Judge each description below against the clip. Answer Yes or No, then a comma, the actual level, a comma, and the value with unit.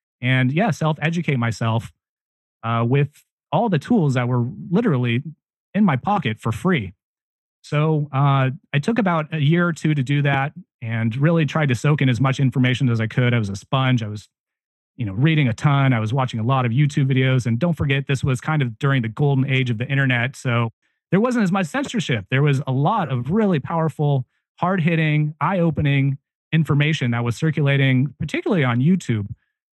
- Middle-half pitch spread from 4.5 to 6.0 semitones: No, average, 3.9 semitones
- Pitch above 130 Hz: Yes, medium, 140 Hz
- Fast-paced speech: No, average, 195 wpm